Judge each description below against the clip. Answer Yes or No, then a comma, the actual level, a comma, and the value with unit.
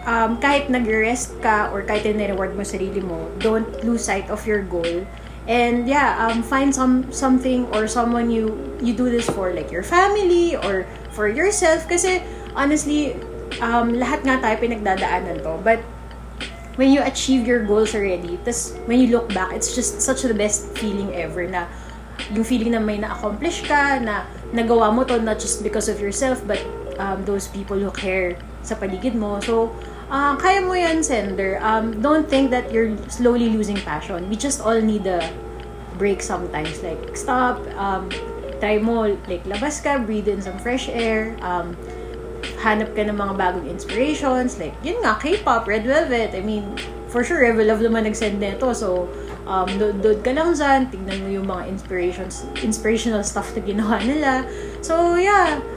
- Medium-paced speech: Yes, average, 175 wpm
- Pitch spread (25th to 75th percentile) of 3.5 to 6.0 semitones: Yes, average, 4.3 semitones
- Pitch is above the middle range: Yes, high, 225 Hz